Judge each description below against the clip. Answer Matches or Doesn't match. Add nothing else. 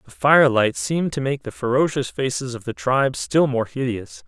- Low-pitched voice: Matches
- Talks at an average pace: Matches